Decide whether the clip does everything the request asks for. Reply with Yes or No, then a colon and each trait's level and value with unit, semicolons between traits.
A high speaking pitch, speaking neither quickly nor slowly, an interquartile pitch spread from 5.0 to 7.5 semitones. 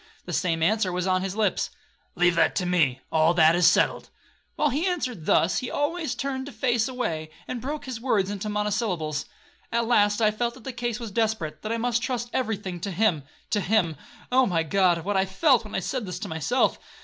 No: high, 210 Hz; fast, 210 wpm; wide, 5.4 semitones